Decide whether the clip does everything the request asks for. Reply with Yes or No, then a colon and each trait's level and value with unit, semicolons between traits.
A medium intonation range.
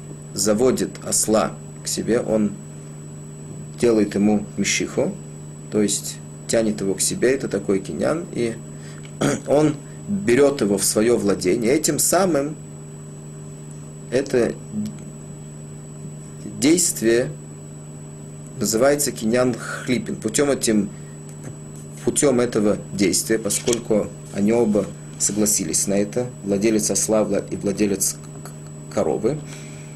No: wide, 6.2 semitones